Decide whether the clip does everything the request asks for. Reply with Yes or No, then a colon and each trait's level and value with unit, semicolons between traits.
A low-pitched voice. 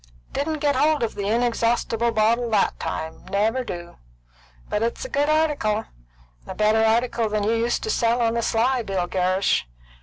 No: high, 230 Hz